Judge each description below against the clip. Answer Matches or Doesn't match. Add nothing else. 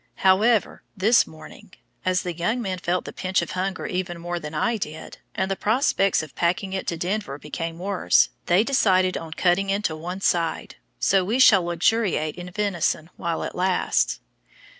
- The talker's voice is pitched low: Doesn't match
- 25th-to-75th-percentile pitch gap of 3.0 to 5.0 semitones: Doesn't match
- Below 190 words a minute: Matches